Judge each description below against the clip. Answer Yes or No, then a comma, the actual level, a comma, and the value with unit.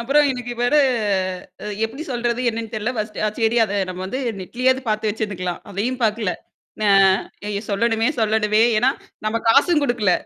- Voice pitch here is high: Yes, high, 225 Hz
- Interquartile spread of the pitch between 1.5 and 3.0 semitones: Yes, average, 2.7 semitones